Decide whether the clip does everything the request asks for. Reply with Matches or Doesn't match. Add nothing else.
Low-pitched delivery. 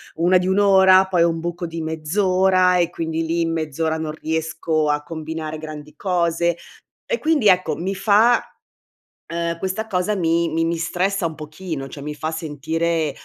Doesn't match